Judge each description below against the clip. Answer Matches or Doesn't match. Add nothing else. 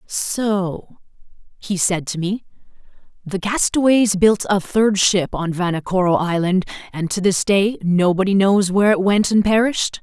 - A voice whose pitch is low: Doesn't match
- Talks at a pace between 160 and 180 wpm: Doesn't match